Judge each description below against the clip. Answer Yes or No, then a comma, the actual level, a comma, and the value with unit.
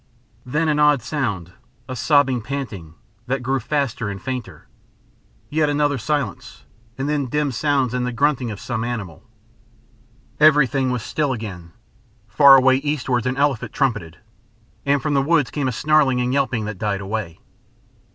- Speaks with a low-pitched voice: Yes, low, 130 Hz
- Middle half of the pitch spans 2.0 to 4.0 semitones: No, average, 4.4 semitones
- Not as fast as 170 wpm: Yes, average, 155 wpm